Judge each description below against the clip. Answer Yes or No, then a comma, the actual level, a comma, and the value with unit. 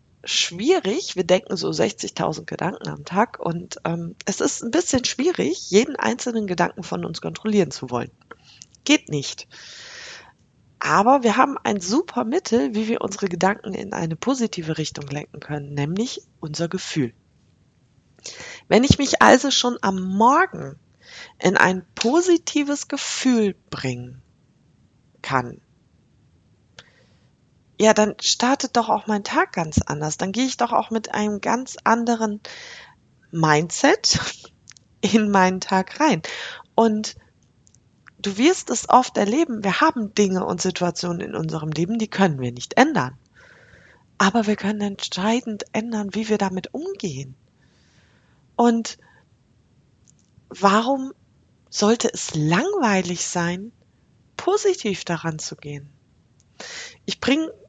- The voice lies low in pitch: No, high, 210 Hz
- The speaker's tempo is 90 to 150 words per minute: Yes, slow, 125 wpm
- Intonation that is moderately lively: No, wide, 6.3 semitones